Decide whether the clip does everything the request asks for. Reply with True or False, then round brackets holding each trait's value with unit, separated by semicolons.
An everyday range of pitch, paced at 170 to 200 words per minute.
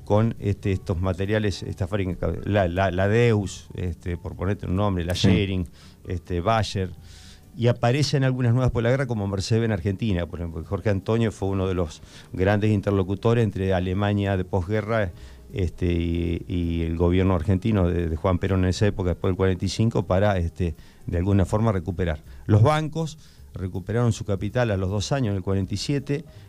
True (3.0 semitones; 175 wpm)